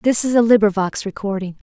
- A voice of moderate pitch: No, high, 210 Hz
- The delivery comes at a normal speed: Yes, average, 180 wpm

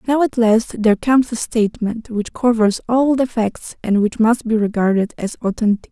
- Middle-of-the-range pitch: No, high, 225 Hz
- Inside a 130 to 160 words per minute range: No, average, 195 wpm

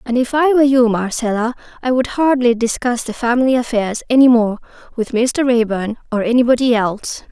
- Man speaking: No, female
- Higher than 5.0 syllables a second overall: Yes, 5.6 syllables/s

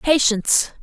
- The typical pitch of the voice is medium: No, very high, 255 Hz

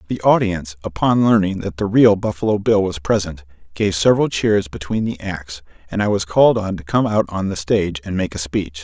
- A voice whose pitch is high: No, very low, 95 Hz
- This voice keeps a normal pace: No, fast, 215 wpm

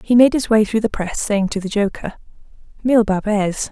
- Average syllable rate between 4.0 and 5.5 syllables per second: No, 6.3 syllables/s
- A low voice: No, high, 215 Hz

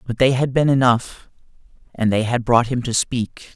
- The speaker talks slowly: No, fast, 205 wpm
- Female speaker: No, male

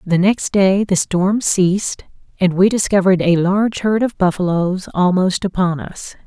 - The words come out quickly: No, average, 165 wpm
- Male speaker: No, female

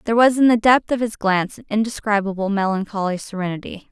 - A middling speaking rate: Yes, average, 185 wpm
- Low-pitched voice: No, high, 210 Hz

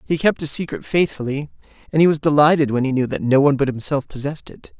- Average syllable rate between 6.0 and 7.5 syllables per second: Yes, 6.7 syllables/s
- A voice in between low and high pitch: Yes, medium, 145 Hz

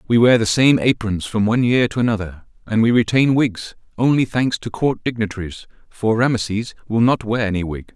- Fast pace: No, average, 195 wpm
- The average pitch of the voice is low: Yes, low, 110 Hz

